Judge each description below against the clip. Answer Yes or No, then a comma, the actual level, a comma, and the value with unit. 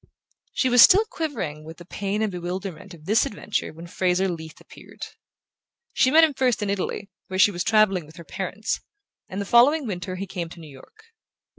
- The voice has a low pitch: No, high, 190 Hz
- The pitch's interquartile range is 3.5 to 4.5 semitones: Yes, average, 4.1 semitones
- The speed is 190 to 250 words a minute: Yes, average, 195 wpm